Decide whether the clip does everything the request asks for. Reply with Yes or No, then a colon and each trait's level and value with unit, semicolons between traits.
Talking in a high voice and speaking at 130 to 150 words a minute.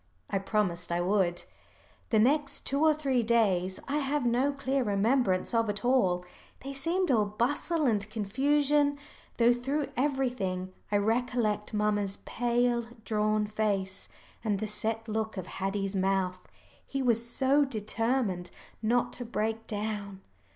Yes: high, 225 Hz; average, 140 wpm